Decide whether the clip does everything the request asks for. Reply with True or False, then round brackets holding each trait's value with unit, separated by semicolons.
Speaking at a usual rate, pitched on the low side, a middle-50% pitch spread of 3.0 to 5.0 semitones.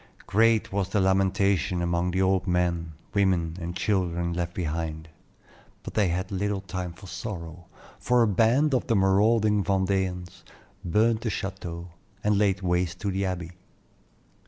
False (145 wpm; 95 Hz; 2.6 semitones)